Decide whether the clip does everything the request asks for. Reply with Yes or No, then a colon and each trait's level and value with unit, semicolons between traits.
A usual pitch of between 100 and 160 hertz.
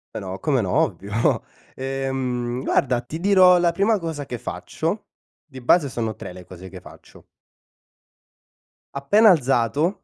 Yes: low, 135 Hz